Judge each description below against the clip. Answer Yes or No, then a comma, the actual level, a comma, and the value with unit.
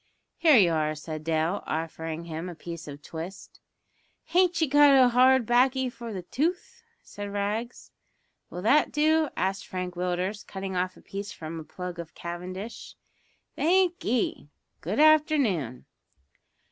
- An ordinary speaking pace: Yes, average, 150 wpm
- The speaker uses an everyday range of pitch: No, wide, 7.6 semitones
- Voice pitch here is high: Yes, high, 195 Hz